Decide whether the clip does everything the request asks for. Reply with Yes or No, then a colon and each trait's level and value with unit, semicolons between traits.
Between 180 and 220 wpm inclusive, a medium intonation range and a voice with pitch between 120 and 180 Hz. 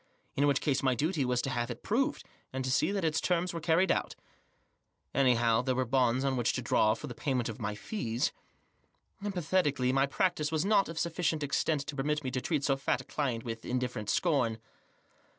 Yes: fast, 205 wpm; average, 4.4 semitones; low, 135 Hz